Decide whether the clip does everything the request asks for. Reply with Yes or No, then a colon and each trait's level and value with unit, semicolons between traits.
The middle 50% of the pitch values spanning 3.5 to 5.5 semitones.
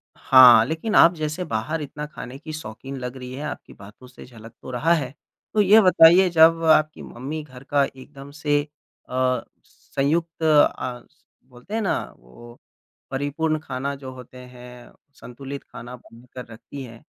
Yes: average, 3.9 semitones